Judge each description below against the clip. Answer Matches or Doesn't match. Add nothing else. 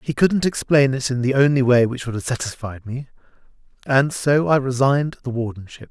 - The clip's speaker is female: Doesn't match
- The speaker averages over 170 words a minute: Matches